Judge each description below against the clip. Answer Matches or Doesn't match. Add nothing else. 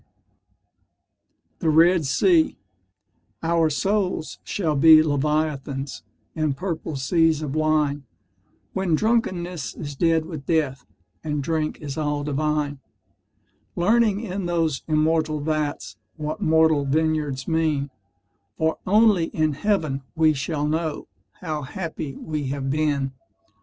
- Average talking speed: Doesn't match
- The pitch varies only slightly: Matches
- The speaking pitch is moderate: Matches